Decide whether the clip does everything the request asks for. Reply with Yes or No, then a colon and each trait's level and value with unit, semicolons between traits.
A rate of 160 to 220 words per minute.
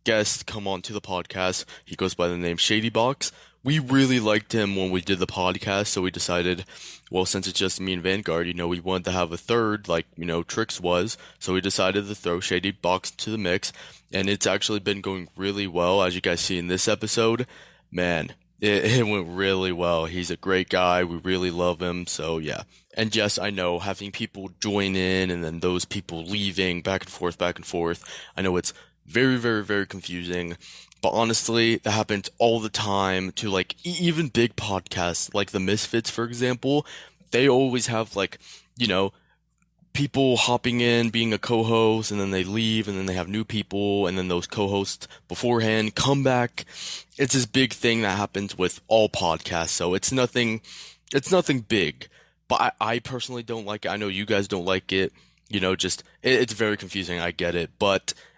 Yes: average, 200 wpm